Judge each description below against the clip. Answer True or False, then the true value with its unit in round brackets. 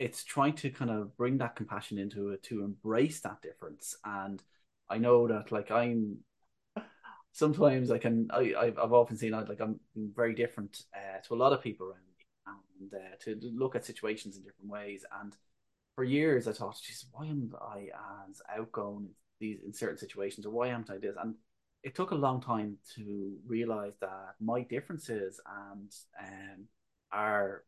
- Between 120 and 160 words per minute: False (180 wpm)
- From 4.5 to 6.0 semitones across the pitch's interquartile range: False (3.0 semitones)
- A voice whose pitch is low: True (110 Hz)